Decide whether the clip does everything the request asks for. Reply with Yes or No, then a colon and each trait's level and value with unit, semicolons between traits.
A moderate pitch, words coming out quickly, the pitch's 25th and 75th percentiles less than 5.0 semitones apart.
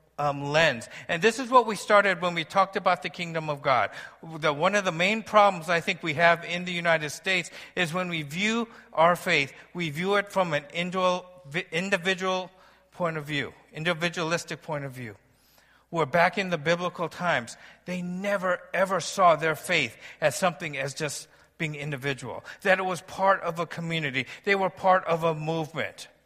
No: medium, 175 Hz; average, 185 wpm; average, 2.8 semitones